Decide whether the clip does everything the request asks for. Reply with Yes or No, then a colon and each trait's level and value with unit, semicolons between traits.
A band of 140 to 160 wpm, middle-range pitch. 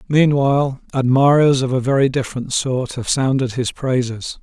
No: average, 150 wpm; low, 130 Hz